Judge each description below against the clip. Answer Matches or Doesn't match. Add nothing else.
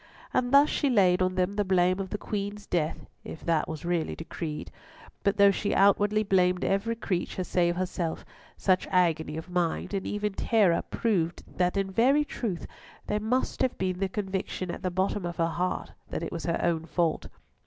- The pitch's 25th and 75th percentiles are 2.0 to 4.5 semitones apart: Matches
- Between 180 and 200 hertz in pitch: Matches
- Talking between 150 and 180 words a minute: Doesn't match